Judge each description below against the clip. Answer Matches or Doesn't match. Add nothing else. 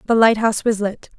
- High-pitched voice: Matches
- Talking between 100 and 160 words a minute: Doesn't match